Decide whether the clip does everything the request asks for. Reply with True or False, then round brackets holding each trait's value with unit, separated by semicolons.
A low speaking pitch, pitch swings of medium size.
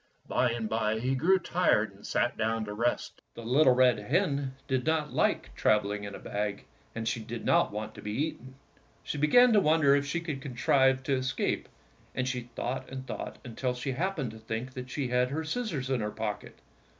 True (130 Hz; 4.1 semitones)